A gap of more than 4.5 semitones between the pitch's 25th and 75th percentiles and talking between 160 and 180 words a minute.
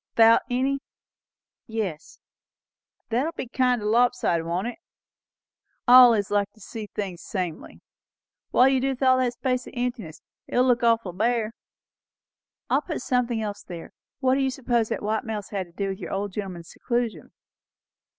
No: average, 3.7 semitones; average, 170 wpm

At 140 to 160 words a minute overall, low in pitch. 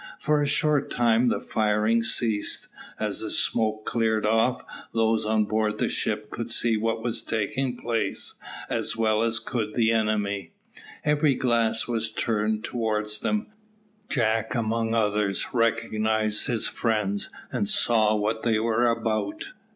Yes: average, 145 wpm; low, 110 Hz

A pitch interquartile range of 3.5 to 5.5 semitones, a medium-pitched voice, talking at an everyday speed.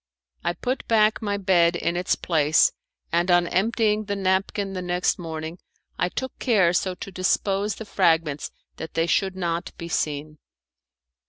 No: average, 3.1 semitones; medium, 180 Hz; average, 160 wpm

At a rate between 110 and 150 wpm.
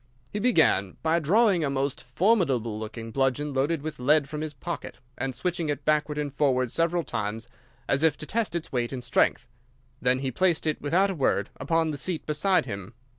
No: average, 195 wpm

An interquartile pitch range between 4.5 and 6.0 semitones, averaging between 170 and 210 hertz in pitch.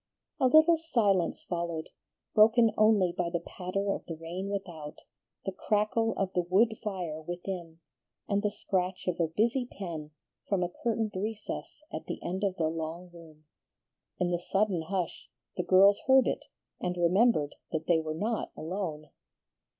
No: average, 3.8 semitones; medium, 185 Hz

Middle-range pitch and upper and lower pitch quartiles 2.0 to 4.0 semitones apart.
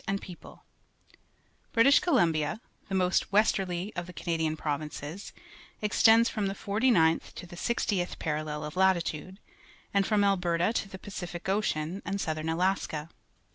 Yes: medium, 180 Hz; average, 3.7 semitones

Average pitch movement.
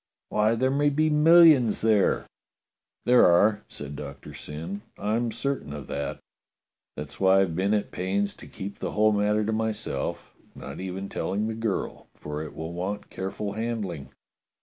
Yes: average, 3.7 semitones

